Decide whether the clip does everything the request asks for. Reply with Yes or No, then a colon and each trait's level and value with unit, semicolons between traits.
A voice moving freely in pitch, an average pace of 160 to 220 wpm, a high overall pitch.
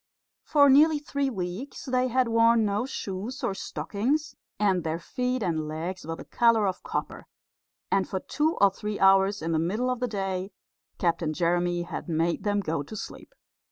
Yes: wide, 6.1 semitones; average, 180 wpm; high, 200 Hz